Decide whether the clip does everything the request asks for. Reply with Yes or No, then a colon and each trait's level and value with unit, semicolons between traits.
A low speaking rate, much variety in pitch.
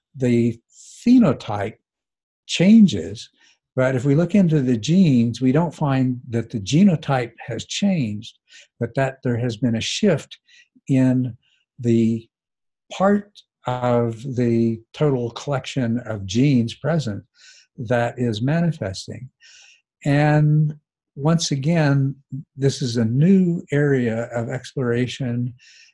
No: slow, 110 wpm; average, 4.6 semitones